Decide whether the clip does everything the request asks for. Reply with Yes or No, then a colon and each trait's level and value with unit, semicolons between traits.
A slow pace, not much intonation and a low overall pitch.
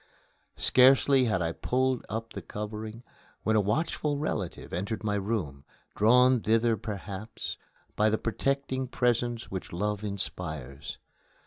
No: slow, 125 wpm; average, 3.7 semitones; low, 110 Hz